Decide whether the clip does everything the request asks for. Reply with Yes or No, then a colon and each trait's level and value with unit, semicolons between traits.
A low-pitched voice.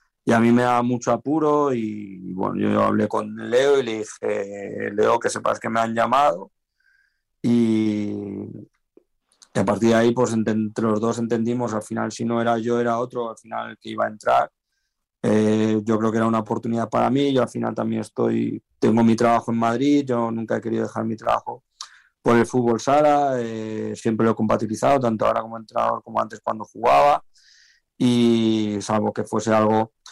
Yes: low, 115 Hz